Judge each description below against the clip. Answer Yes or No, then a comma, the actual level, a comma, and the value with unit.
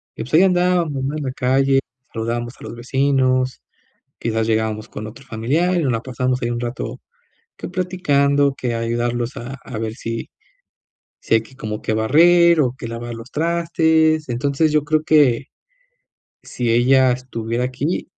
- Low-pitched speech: Yes, low, 130 Hz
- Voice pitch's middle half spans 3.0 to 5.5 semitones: Yes, average, 4.3 semitones